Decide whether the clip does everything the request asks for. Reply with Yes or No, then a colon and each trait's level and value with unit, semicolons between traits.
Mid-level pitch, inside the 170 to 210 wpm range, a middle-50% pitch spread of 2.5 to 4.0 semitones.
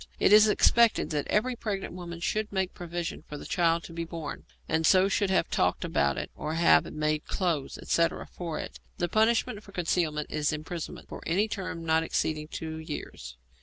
Yes: medium, 170 Hz; average, 195 wpm; average, 3.7 semitones